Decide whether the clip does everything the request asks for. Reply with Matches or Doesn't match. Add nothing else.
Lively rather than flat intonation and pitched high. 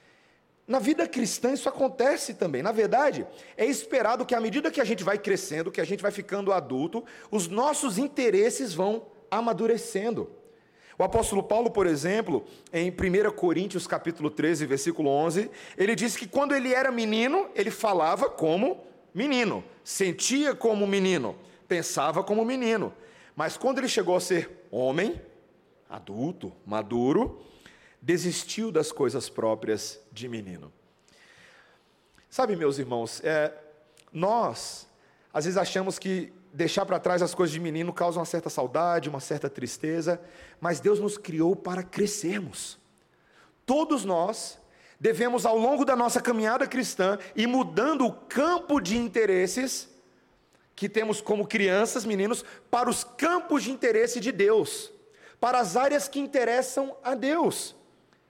Matches